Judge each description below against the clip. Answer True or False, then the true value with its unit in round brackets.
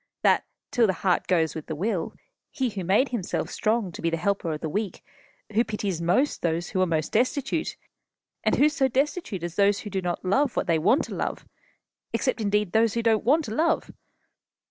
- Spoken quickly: True (210 wpm)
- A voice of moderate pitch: False (205 Hz)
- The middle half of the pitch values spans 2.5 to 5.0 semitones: False (5.5 semitones)